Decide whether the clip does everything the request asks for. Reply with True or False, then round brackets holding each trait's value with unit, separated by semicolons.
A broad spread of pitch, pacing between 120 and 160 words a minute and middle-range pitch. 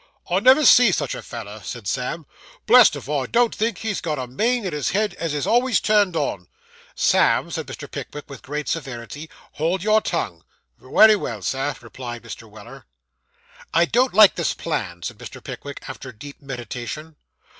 False (8.7 semitones; 175 wpm; 150 Hz)